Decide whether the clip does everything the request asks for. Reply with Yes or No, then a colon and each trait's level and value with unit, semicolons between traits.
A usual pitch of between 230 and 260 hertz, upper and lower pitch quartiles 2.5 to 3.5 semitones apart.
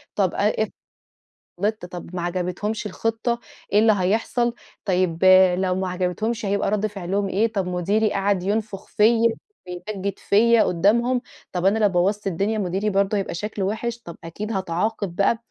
No: high, 200 Hz; average, 3.0 semitones